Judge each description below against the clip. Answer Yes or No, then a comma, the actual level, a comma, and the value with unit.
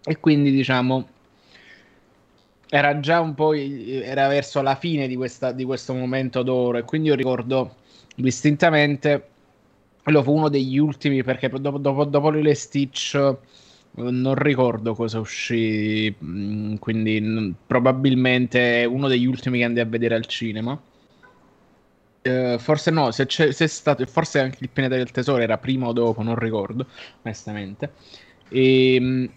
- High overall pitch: No, low, 130 Hz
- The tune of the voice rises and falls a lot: No, average, 3.1 semitones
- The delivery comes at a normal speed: Yes, average, 145 wpm